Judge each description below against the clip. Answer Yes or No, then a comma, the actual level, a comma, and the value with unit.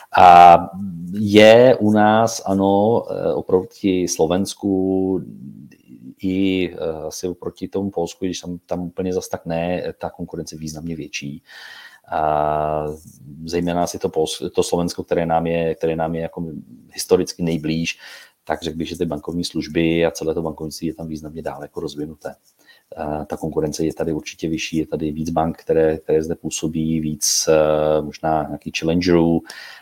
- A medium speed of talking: Yes, average, 155 wpm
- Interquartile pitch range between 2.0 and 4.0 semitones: Yes, narrow, 2.4 semitones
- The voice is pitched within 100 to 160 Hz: No, very low, 85 Hz